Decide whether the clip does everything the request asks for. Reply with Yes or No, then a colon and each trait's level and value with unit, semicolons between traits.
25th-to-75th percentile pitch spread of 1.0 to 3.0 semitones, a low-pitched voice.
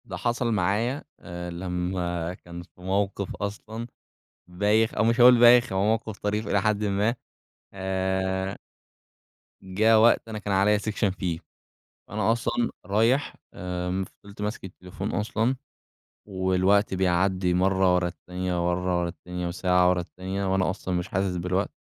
Yes: average, 2.7 semitones; very low, 95 Hz